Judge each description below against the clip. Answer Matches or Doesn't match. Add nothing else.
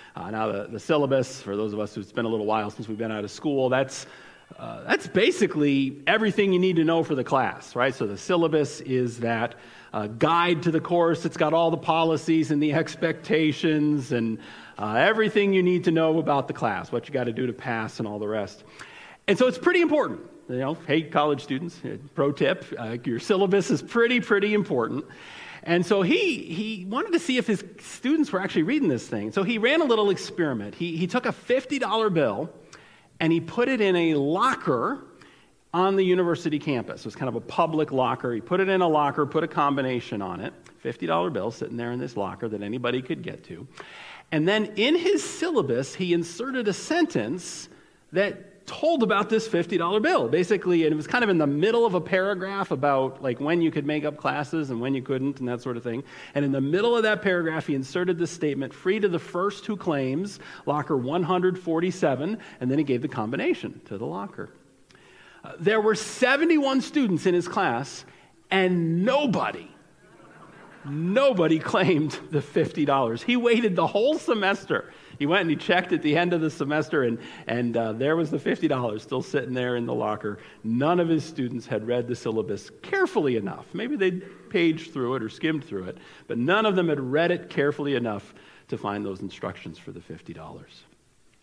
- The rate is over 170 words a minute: Matches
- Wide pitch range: Matches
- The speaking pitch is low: Doesn't match